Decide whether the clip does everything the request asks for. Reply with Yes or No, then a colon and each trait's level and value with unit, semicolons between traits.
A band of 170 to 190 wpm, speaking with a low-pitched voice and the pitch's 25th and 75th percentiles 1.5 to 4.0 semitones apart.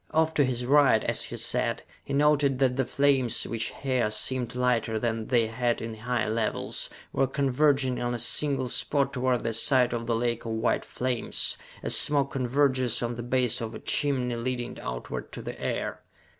Yes: average, 185 wpm; low, 125 Hz; narrow, 2.5 semitones